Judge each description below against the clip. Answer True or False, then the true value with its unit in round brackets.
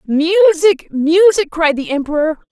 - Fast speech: False (120 wpm)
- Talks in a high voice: True (330 Hz)